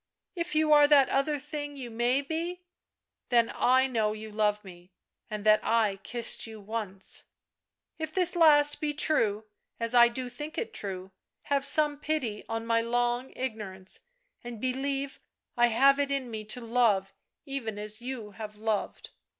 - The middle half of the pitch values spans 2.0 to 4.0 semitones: No, average, 4.7 semitones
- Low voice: No, high, 240 Hz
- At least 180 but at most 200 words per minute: No, average, 170 wpm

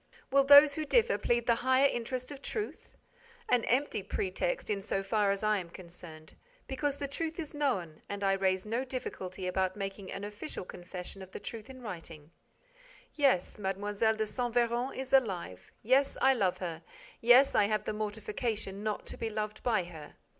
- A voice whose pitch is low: No, high, 215 Hz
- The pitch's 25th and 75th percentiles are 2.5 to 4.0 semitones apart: No, average, 5.3 semitones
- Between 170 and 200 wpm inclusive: Yes, average, 180 wpm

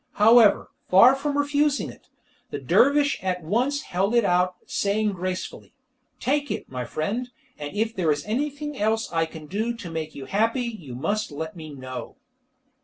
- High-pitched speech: Yes, high, 205 Hz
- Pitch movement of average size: No, wide, 7.2 semitones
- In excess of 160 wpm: Yes, average, 170 wpm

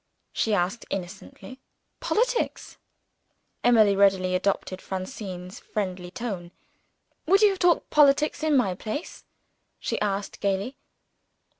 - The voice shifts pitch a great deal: Yes, wide, 6.7 semitones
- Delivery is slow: Yes, slow, 110 wpm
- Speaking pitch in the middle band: No, high, 205 Hz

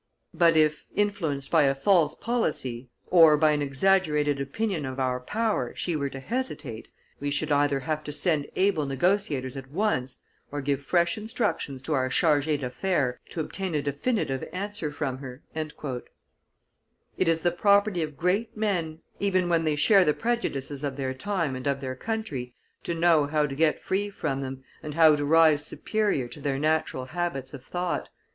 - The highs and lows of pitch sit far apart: No, average, 4.7 semitones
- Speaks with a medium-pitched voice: Yes, medium, 150 Hz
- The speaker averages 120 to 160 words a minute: No, average, 175 wpm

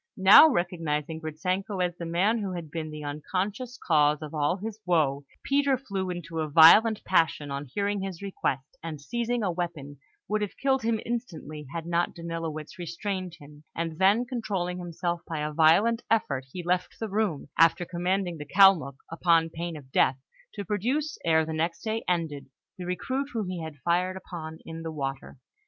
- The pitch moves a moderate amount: Yes, average, 4.2 semitones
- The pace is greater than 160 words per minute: Yes, average, 180 wpm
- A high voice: No, medium, 175 Hz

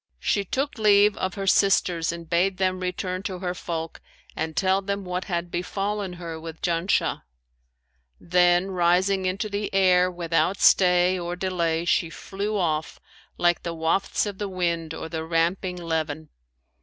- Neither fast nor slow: Yes, average, 155 wpm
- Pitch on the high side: No, medium, 180 Hz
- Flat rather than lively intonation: Yes, narrow, 2.3 semitones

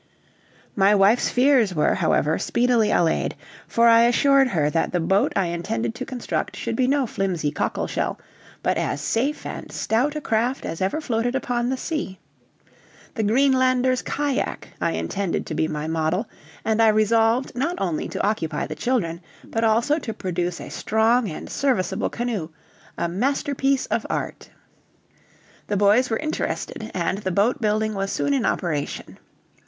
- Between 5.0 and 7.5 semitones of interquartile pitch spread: Yes, wide, 5.4 semitones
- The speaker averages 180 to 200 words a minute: No, average, 160 wpm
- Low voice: No, high, 225 Hz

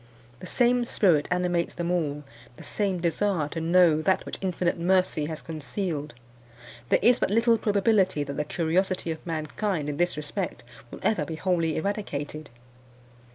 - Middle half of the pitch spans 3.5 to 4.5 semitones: Yes, average, 3.8 semitones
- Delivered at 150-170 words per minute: Yes, average, 155 wpm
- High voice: No, medium, 175 Hz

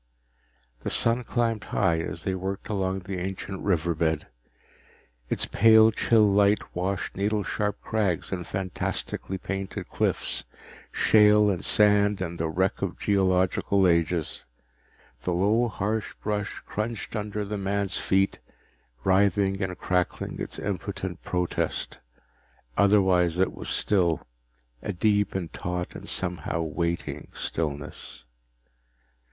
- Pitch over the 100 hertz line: No, very low, 95 Hz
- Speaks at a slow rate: Yes, slow, 125 wpm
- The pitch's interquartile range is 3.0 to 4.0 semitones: No, narrow, 2.6 semitones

